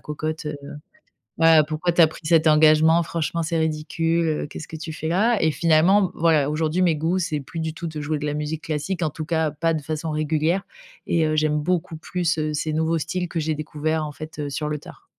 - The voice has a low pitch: No, medium, 160 Hz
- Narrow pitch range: Yes, narrow, 1.5 semitones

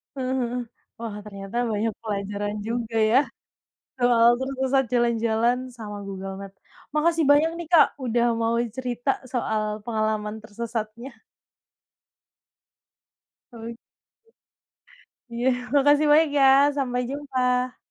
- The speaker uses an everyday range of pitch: Yes, average, 3.2 semitones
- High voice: Yes, high, 240 Hz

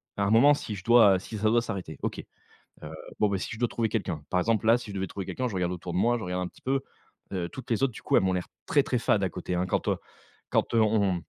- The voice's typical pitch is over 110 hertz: No, low, 100 Hz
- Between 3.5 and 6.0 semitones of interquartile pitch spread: Yes, average, 4.2 semitones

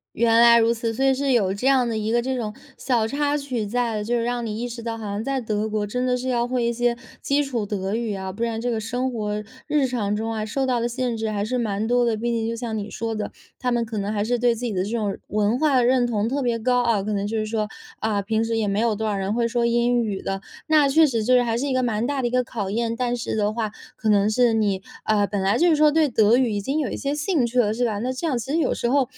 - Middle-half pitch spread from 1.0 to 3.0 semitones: Yes, average, 2.7 semitones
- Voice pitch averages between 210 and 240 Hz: Yes, high, 235 Hz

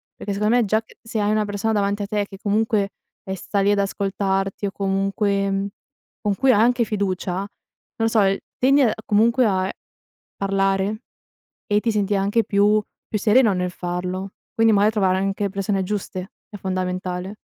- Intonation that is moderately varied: No, narrow, 1.7 semitones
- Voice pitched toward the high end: Yes, high, 200 Hz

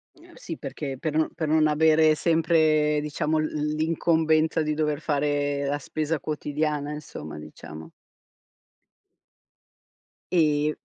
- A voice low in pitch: No, medium, 155 Hz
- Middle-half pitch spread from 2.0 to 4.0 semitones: No, narrow, 1.4 semitones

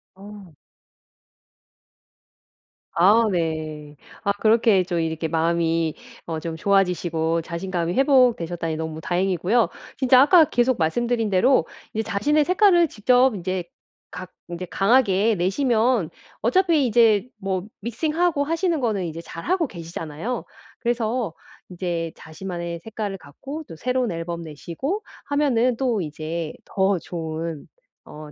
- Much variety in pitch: Yes, wide, 6.8 semitones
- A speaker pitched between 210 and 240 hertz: No, high, 195 Hz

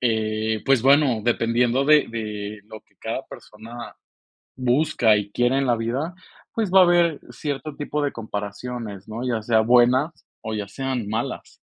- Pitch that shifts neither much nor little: Yes, average, 3.9 semitones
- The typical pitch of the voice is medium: No, low, 120 Hz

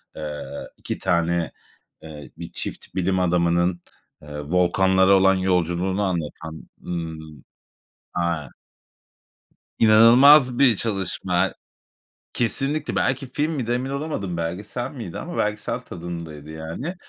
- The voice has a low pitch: Yes, very low, 90 Hz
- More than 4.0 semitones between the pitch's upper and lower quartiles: Yes, wide, 5.4 semitones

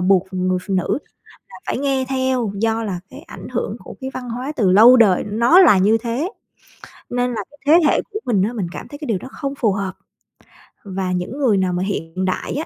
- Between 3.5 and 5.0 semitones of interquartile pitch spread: No, wide, 5.5 semitones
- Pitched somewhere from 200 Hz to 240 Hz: Yes, high, 225 Hz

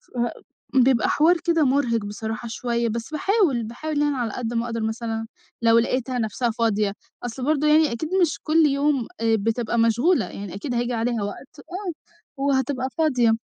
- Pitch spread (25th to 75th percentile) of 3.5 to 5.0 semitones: Yes, average, 4.1 semitones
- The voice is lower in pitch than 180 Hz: No, high, 245 Hz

